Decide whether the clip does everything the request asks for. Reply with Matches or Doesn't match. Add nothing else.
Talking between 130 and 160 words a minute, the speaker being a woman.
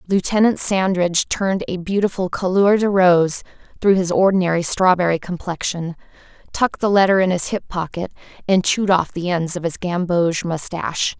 Matches